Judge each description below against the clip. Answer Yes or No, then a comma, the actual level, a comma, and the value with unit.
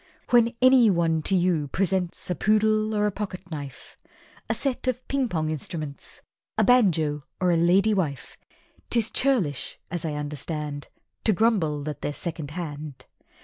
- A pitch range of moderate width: No, wide, 6.1 semitones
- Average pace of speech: Yes, average, 145 wpm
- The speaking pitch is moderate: Yes, medium, 175 Hz